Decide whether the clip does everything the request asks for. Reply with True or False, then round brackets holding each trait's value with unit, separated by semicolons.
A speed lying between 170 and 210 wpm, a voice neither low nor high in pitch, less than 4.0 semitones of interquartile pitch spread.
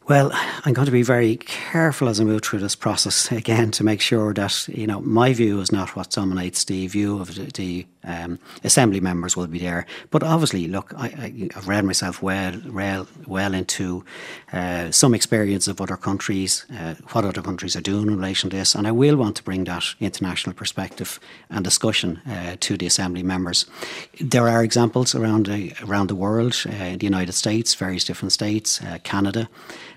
False (195 wpm; 100 Hz; 3.5 semitones)